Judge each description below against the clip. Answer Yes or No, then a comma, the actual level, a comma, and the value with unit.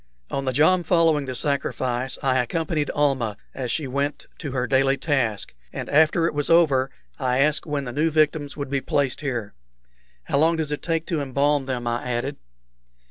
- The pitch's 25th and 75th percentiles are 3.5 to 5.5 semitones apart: No, average, 2.9 semitones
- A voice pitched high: No, medium, 140 Hz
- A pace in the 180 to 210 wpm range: Yes, average, 190 wpm